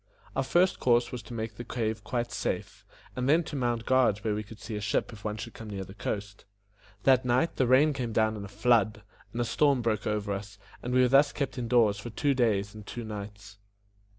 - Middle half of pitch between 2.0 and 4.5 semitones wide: Yes, average, 3.1 semitones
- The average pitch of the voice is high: No, low, 115 Hz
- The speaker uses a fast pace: Yes, fast, 235 wpm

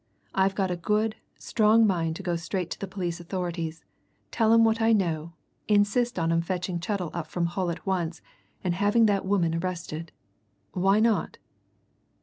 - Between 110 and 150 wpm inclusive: No, average, 170 wpm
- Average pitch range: Yes, average, 3.3 semitones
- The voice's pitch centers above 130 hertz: Yes, medium, 185 Hz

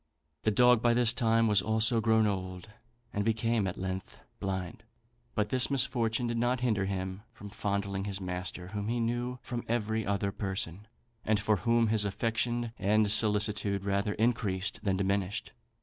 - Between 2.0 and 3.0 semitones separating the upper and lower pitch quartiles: Yes, average, 2.7 semitones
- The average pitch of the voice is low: Yes, low, 105 Hz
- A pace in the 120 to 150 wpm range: No, average, 165 wpm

